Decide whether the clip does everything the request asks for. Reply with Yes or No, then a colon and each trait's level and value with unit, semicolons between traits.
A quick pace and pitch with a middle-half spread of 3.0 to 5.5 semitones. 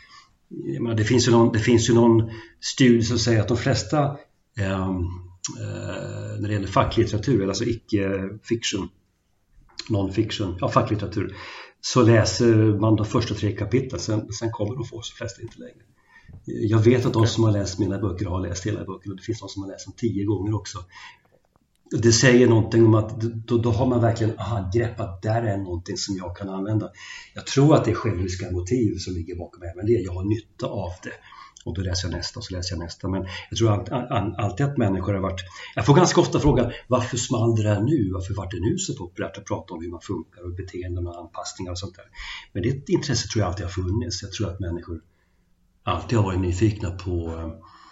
Yes: fast, 215 wpm; average, 3.7 semitones